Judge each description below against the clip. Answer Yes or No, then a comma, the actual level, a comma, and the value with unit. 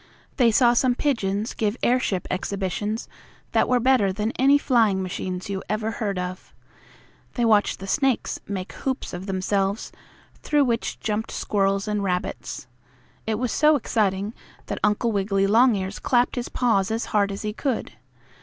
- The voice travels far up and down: No, average, 3.7 semitones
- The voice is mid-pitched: No, high, 210 Hz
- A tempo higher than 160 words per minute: No, average, 155 wpm